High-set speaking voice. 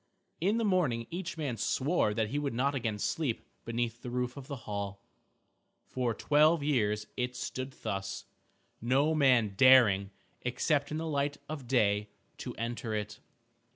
No: low, 125 Hz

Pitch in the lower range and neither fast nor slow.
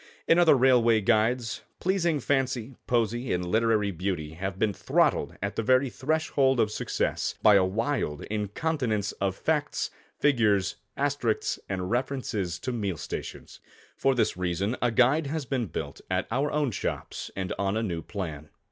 Yes: low, 115 Hz; average, 155 wpm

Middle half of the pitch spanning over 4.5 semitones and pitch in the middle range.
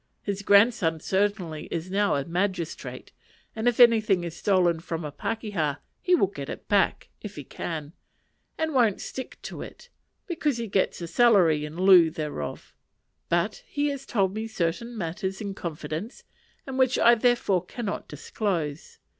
No: wide, 5.5 semitones; high, 195 Hz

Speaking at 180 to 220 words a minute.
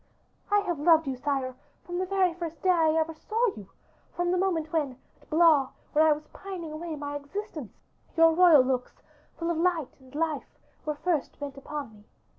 Yes: average, 195 wpm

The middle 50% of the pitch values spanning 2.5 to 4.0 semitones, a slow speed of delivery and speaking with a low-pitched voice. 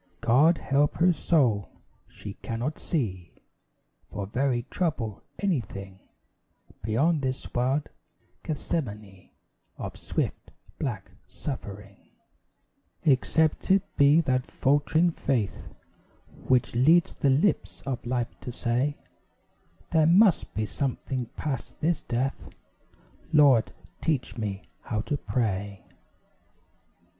No: average, 5.3 semitones; slow, 100 wpm; low, 130 Hz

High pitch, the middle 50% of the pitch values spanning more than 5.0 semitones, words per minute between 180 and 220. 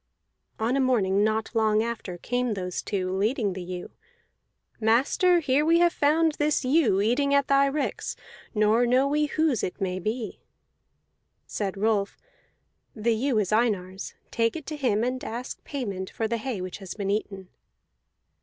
No: high, 225 Hz; wide, 5.4 semitones; average, 165 wpm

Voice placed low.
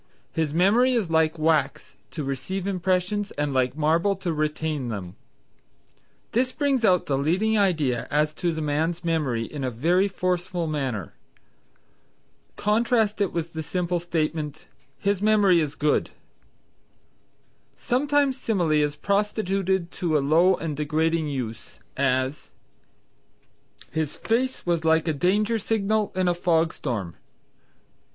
No: medium, 165 Hz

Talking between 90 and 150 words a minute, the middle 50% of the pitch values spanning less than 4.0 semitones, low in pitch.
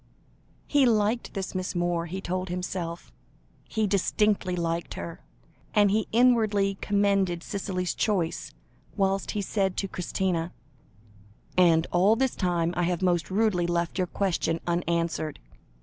No: slow, 135 wpm; average, 2.8 semitones; medium, 185 Hz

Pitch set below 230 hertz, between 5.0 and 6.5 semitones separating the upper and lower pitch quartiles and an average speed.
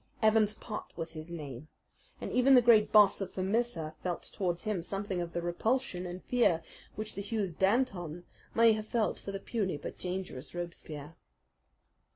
No: high, 190 Hz; average, 4.0 semitones; average, 170 wpm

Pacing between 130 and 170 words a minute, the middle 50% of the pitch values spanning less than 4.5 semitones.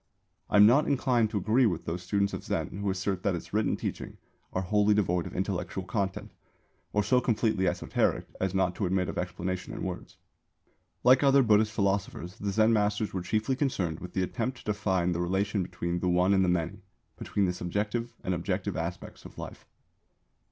No: average, 195 wpm; average, 3.0 semitones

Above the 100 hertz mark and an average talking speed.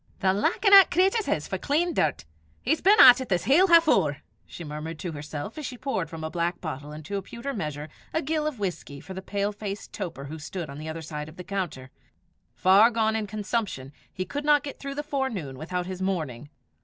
No: high, 190 Hz; fast, 225 wpm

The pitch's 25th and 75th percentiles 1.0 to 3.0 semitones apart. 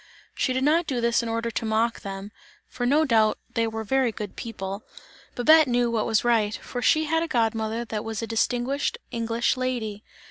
Yes: narrow, 2.5 semitones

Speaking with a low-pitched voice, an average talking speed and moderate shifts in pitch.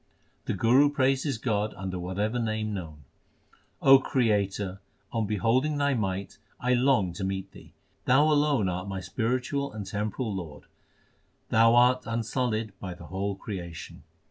Yes: low, 110 Hz; average, 145 wpm; average, 4.9 semitones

